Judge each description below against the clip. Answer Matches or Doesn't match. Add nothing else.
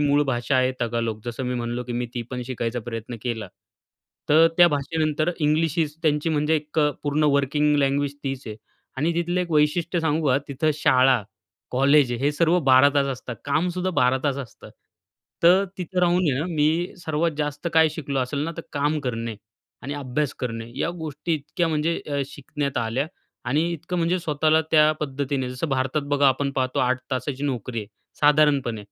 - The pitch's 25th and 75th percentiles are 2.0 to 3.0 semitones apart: Doesn't match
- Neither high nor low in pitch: Matches